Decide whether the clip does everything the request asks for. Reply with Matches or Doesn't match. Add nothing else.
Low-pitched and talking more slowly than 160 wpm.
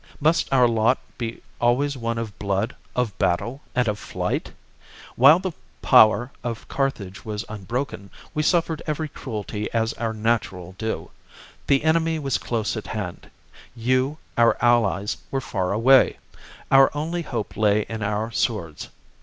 Matches